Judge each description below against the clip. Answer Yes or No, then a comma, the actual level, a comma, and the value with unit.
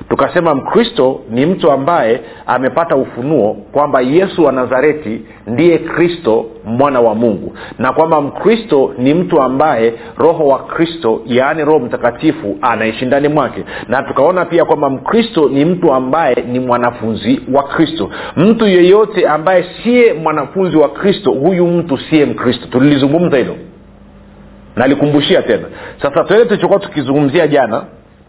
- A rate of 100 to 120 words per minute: No, average, 135 wpm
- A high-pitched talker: No, medium, 150 Hz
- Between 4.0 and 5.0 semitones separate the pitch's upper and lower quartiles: No, wide, 5.4 semitones